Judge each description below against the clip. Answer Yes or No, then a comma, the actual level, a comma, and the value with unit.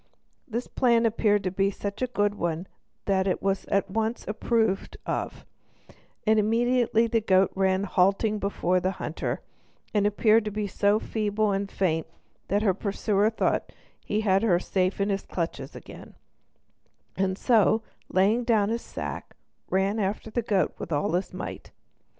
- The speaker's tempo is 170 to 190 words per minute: No, average, 155 wpm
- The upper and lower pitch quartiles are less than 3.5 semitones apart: Yes, narrow, 2.4 semitones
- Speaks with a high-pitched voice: Yes, high, 205 Hz